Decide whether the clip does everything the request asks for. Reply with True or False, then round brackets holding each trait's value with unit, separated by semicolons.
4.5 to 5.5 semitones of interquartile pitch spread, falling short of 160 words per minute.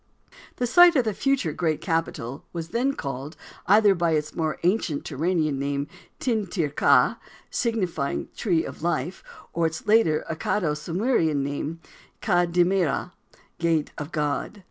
True (5.0 semitones; 145 wpm)